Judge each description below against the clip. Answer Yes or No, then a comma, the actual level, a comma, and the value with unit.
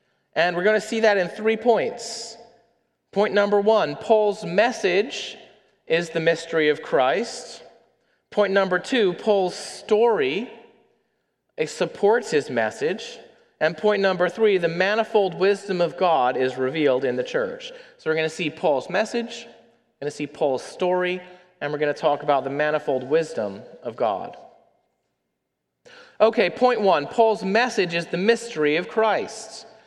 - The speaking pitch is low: No, high, 205 Hz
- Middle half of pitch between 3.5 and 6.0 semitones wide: Yes, average, 5.3 semitones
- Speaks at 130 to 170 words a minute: Yes, average, 150 wpm